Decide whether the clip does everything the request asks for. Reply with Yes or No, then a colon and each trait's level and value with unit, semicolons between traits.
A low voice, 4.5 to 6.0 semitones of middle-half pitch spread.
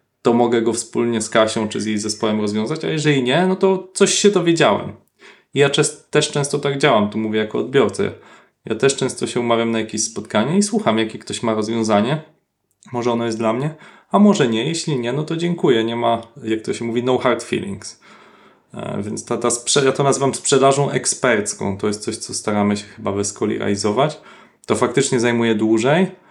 Yes: low, 120 Hz; average, 5.0 semitones